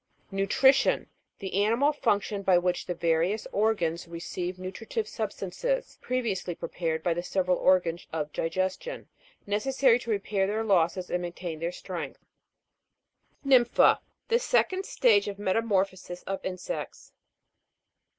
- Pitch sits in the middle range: No, high, 195 Hz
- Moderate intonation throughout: Yes, average, 4.3 semitones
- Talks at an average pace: No, slow, 130 wpm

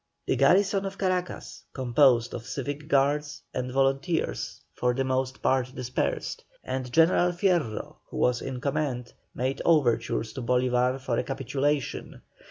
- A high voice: No, low, 135 Hz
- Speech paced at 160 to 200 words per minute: No, average, 140 wpm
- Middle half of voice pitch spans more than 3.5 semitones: No, average, 3.0 semitones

